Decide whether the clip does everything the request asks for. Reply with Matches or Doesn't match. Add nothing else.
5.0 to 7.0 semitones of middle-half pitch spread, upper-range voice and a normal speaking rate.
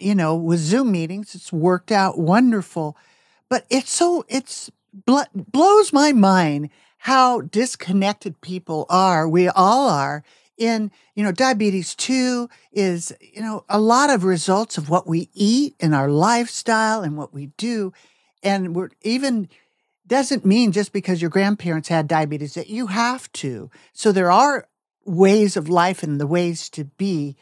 Matches